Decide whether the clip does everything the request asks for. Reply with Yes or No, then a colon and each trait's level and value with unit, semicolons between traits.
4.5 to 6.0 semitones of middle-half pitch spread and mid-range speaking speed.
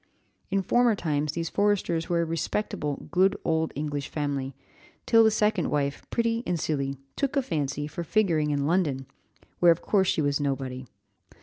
Yes: average, 5.2 semitones; average, 170 wpm